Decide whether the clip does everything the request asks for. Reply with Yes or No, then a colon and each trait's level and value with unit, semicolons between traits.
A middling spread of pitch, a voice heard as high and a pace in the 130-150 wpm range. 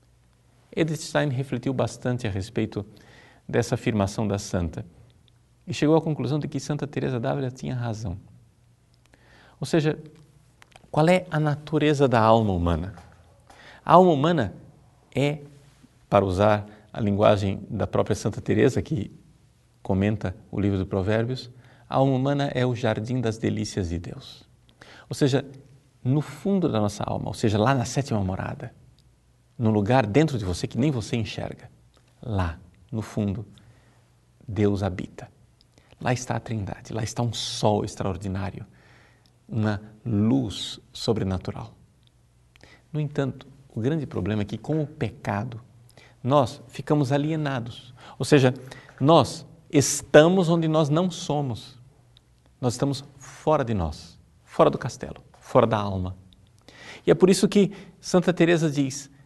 No: average, 4.8 semitones; low, 125 Hz; average, 140 wpm